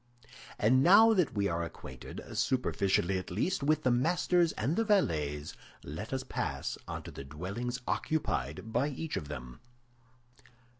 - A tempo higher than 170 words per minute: No, average, 150 wpm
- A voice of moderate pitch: No, low, 120 Hz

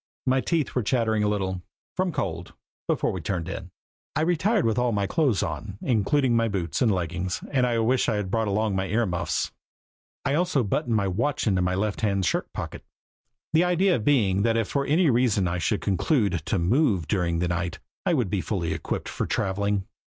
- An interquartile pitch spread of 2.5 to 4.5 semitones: No, wide, 5.4 semitones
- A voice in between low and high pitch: No, low, 105 Hz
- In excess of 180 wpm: Yes, average, 195 wpm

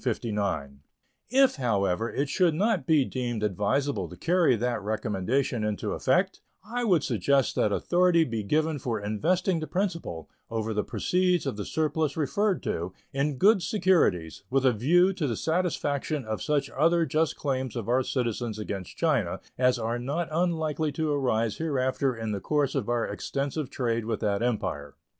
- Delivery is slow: No, average, 165 wpm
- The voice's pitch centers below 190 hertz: Yes, low, 135 Hz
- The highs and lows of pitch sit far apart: Yes, wide, 6.4 semitones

